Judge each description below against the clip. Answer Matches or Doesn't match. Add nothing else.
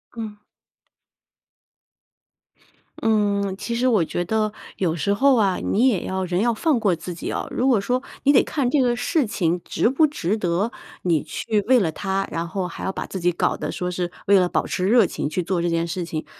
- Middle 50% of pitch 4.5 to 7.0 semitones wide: Matches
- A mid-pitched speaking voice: Doesn't match